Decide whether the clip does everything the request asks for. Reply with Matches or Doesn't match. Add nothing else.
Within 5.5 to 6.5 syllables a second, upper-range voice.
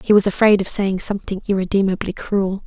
Matches